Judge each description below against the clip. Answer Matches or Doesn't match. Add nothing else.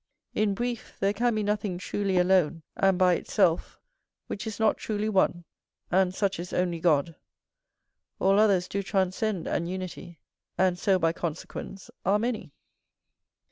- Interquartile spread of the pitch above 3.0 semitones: Doesn't match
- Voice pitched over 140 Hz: Matches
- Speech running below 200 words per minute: Matches